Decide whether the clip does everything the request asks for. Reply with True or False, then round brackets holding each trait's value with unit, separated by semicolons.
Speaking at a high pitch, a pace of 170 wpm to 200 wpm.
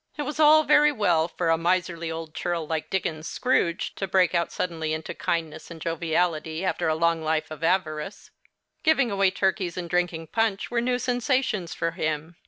False (170 Hz; 185 wpm)